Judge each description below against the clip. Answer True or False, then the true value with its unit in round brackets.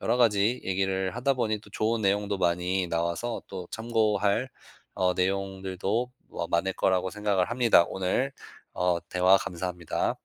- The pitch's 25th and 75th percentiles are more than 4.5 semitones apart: False (3.1 semitones)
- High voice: False (95 Hz)